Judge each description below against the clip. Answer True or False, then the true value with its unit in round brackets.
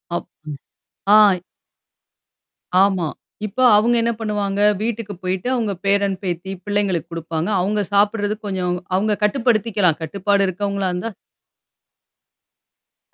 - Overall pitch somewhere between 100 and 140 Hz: False (200 Hz)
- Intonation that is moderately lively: False (2.3 semitones)